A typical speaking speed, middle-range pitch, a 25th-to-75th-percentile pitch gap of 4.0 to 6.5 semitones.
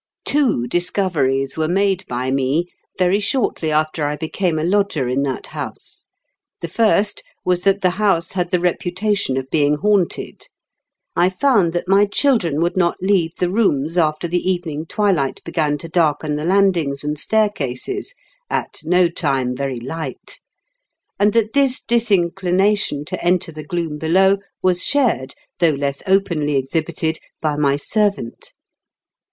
Yes: average, 150 wpm; medium, 170 Hz; average, 4.8 semitones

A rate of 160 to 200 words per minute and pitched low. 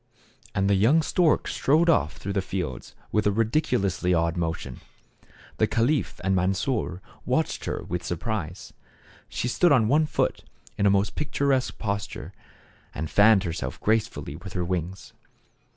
No: average, 150 wpm; low, 100 Hz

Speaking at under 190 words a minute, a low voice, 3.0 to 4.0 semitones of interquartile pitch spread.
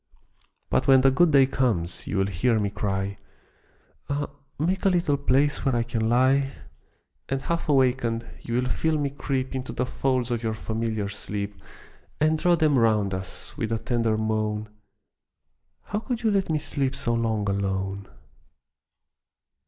No: average, 160 wpm; low, 125 Hz; average, 4.5 semitones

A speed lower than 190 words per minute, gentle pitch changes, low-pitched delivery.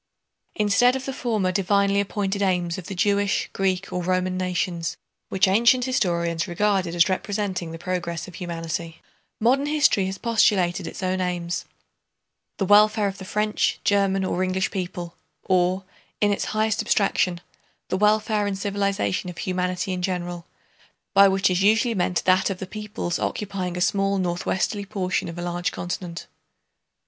No: average, 155 wpm; narrow, 2.3 semitones; high, 190 Hz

